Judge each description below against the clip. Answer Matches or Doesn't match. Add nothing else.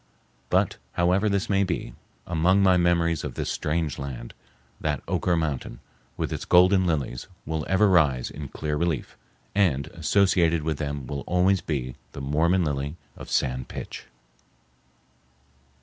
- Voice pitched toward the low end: Matches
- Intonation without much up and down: Doesn't match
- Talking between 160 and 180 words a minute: Doesn't match